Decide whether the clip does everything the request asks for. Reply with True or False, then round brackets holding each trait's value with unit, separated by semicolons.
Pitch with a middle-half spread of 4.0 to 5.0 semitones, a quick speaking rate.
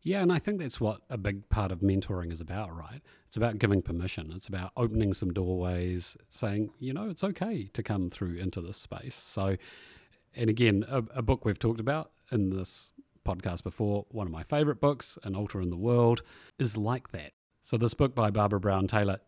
True (4.5 semitones; 210 wpm)